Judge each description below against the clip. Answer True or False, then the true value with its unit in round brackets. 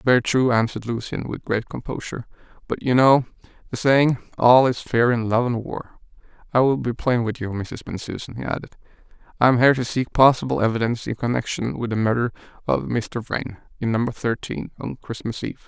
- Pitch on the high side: False (120 Hz)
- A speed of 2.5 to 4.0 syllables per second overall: False (5.8 syllables/s)